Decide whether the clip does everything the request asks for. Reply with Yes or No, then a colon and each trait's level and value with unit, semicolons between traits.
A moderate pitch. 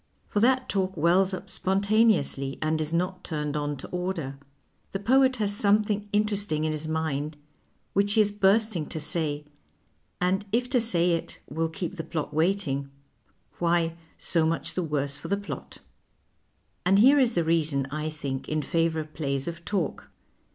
Yes: medium, 170 Hz